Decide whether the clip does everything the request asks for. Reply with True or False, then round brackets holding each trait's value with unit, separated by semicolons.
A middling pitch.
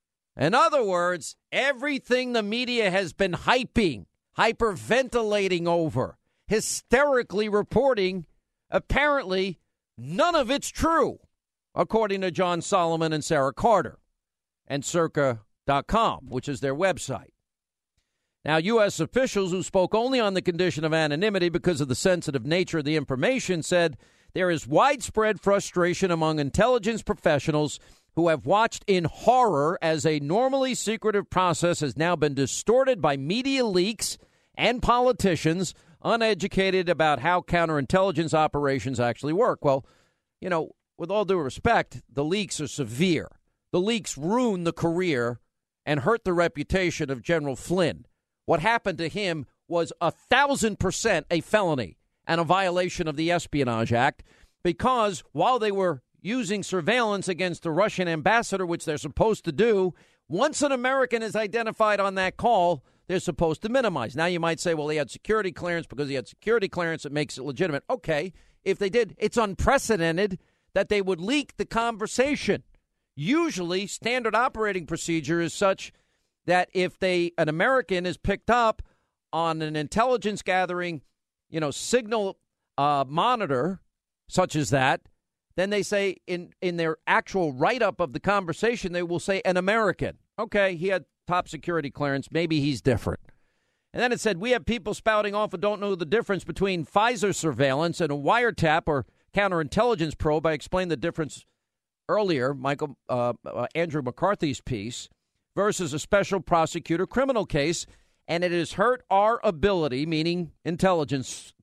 True (180 Hz)